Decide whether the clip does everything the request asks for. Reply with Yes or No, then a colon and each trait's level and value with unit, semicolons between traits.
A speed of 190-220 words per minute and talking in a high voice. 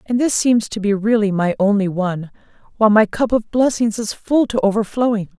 Yes: average, 200 wpm; high, 215 Hz